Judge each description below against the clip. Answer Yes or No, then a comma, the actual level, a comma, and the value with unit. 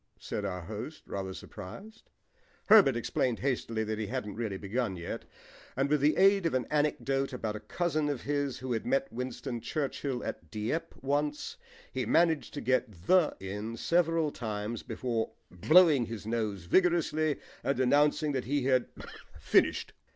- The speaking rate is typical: Yes, average, 160 wpm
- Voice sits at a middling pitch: No, low, 130 Hz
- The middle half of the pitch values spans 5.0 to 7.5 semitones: Yes, wide, 5.6 semitones